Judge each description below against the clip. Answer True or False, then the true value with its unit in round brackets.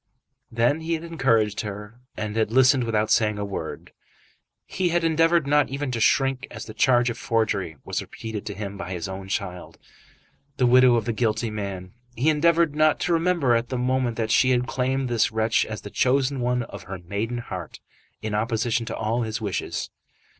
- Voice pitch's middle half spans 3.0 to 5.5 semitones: True (3.9 semitones)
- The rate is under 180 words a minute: False (195 wpm)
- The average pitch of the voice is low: True (120 Hz)